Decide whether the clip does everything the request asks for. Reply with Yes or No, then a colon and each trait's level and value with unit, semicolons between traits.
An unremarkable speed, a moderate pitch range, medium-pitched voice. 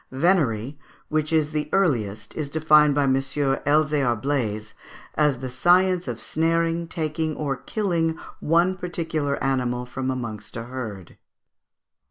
No: slow, 130 wpm; average, 4.5 semitones; medium, 145 Hz